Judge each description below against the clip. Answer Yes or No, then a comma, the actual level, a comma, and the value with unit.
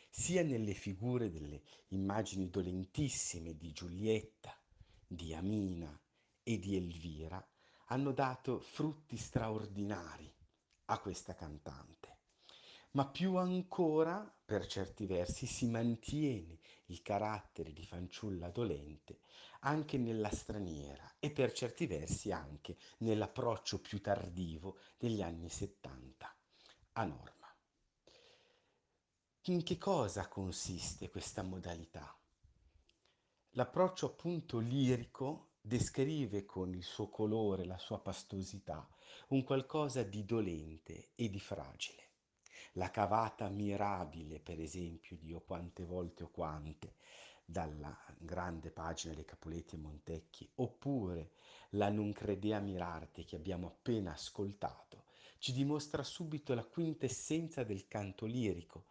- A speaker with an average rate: No, slow, 110 wpm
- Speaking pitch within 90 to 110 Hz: Yes, low, 100 Hz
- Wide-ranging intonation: Yes, wide, 6.0 semitones